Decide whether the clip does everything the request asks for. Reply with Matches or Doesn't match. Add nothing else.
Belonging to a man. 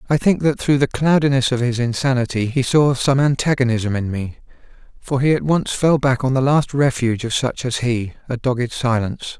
Matches